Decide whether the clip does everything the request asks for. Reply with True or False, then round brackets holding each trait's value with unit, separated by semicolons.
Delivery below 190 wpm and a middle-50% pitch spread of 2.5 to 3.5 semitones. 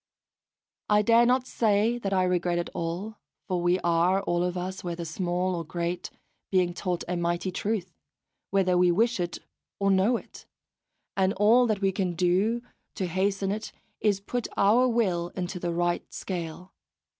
True (170 wpm; 2.9 semitones)